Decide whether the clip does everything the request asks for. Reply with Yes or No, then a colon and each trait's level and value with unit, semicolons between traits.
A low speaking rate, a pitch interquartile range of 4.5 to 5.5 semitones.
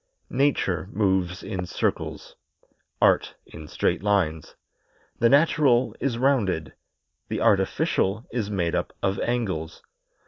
Yes: slow, 110 wpm; average, 5.2 semitones